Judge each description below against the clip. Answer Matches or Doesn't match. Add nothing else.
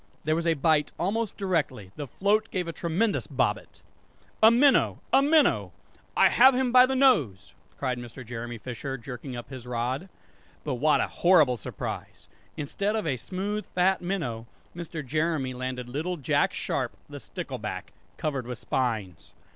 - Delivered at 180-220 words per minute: Doesn't match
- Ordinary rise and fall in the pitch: Doesn't match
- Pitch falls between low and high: Matches